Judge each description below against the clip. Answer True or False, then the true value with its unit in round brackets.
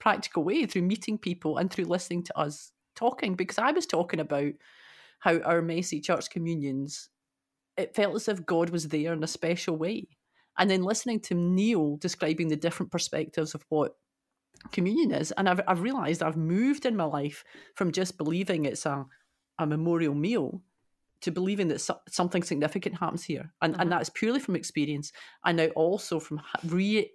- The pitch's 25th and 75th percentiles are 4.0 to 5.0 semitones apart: False (3.2 semitones)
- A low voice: False (175 Hz)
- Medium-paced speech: True (175 wpm)